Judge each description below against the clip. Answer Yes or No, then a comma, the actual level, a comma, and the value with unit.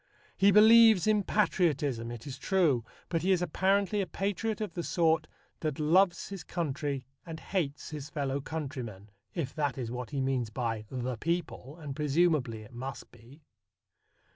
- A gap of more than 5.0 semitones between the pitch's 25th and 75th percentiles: Yes, wide, 5.6 semitones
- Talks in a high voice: No, medium, 150 Hz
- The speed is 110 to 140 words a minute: No, average, 165 wpm